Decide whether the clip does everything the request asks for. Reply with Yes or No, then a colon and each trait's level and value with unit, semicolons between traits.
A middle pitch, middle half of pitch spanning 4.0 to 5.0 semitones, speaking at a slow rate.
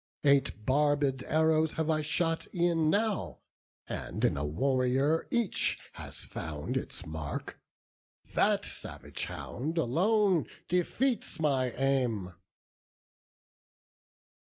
Yes: medium, 150 Hz; average, 4.3 semitones; slow, 100 wpm